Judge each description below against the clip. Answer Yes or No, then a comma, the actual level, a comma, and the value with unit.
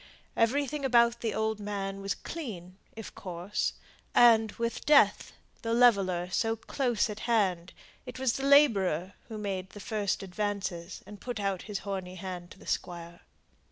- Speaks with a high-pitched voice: Yes, high, 205 Hz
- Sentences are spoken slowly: No, average, 155 wpm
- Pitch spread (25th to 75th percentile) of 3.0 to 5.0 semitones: Yes, average, 3.8 semitones